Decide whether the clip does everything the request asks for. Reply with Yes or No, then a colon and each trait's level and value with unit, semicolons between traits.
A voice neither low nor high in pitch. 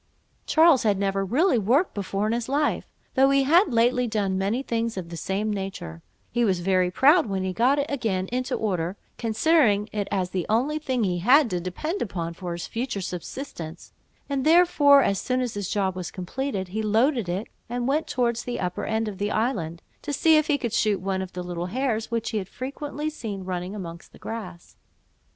No: high, 215 Hz